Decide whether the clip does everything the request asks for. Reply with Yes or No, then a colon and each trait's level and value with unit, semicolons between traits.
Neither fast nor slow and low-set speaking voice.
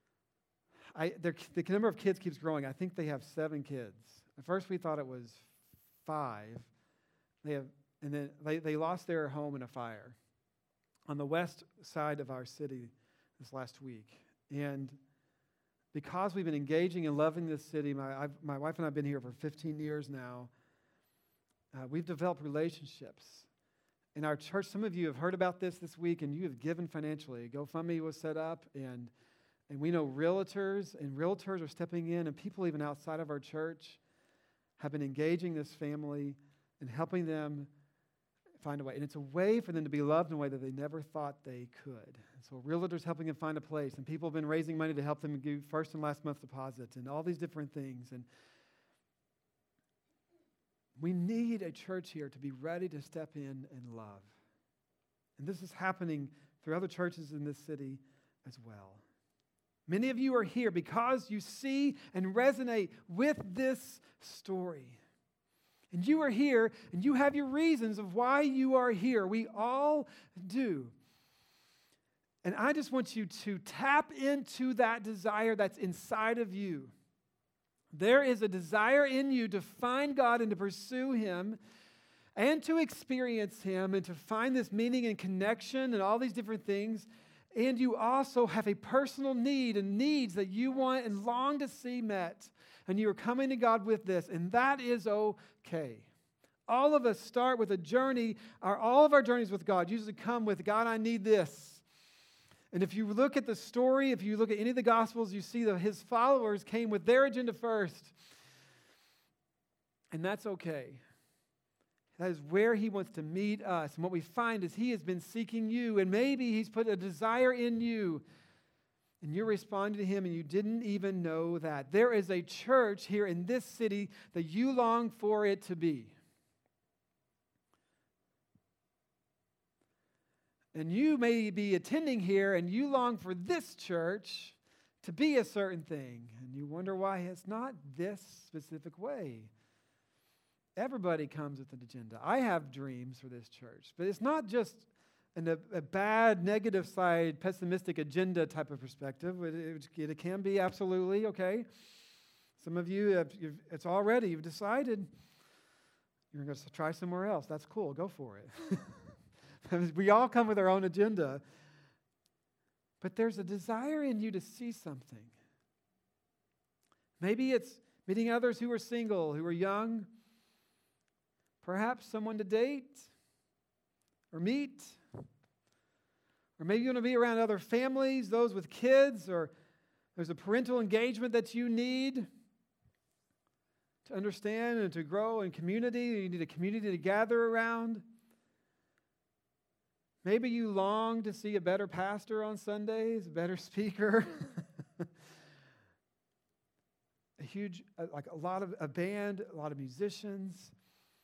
No: average, 170 wpm; medium, 185 Hz